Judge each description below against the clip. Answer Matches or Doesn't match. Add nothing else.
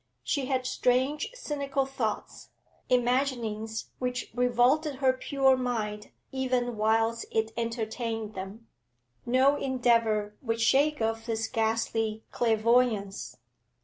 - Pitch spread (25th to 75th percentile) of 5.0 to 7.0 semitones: Doesn't match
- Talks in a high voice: Matches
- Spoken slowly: Matches